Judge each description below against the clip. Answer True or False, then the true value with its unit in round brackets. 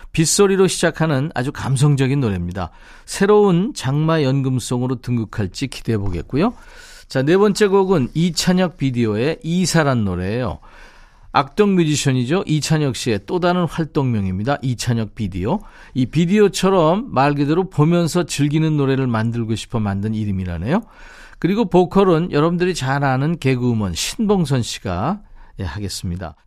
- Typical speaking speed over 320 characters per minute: True (335 characters per minute)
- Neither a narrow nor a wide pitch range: False (7.1 semitones)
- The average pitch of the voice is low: False (145 Hz)